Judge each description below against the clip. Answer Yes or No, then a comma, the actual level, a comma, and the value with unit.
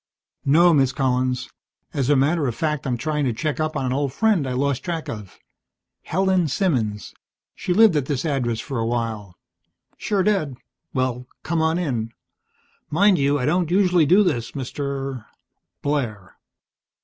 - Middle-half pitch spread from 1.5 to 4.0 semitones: No, average, 4.7 semitones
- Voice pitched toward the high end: No, medium, 140 Hz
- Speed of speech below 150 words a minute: No, average, 165 wpm